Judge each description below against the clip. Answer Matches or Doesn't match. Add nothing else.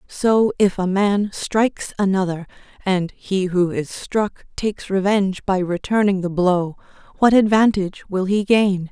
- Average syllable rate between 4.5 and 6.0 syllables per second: Doesn't match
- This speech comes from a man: Doesn't match